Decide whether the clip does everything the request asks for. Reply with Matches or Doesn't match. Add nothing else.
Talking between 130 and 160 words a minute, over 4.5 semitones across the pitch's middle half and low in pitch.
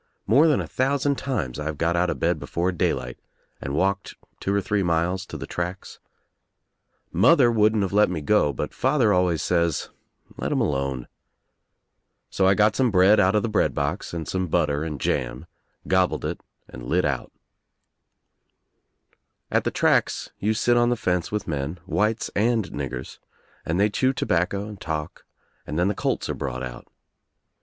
Doesn't match